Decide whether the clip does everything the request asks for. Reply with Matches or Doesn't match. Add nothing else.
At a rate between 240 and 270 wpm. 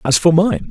Matches